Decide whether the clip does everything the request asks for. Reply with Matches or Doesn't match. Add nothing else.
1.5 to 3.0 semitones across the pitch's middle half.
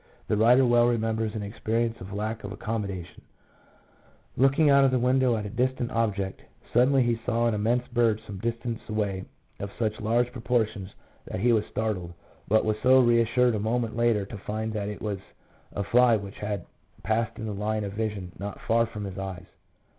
Matches